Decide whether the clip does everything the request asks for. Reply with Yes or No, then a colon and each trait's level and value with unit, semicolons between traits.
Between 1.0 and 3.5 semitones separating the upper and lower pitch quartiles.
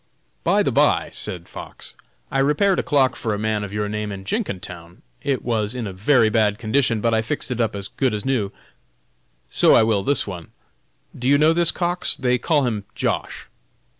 No: average, 4.7 semitones